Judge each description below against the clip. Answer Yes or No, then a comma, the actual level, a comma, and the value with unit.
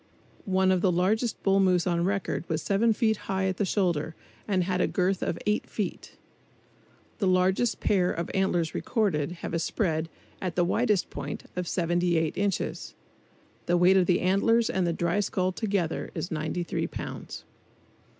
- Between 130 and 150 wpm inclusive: No, average, 170 wpm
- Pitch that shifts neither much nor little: No, narrow, 2.3 semitones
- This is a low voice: No, medium, 185 Hz